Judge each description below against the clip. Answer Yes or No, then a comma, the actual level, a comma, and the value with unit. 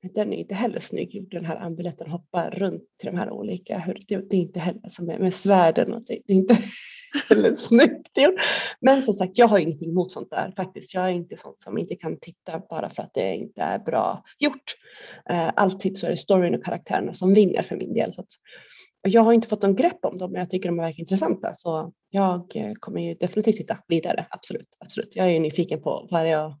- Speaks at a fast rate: Yes, fast, 230 wpm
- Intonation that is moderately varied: Yes, average, 3.6 semitones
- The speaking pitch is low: No, high, 190 Hz